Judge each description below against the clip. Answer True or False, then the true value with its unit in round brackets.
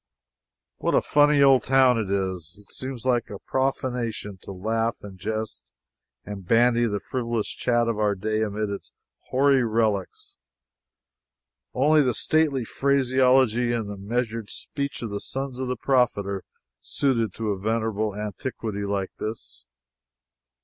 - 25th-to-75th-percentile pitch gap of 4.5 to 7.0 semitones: False (4.0 semitones)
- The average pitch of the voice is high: False (115 Hz)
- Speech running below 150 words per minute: True (140 wpm)